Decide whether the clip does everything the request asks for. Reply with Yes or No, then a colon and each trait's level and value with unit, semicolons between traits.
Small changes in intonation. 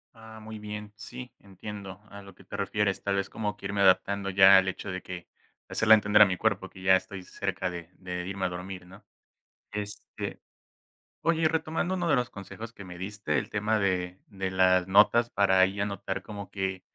Yes: narrow, 2.0 semitones